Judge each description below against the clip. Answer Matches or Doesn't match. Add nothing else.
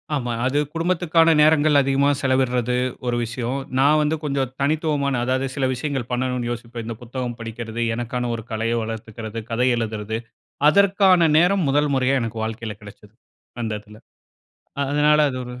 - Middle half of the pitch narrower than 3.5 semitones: Doesn't match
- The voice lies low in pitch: Matches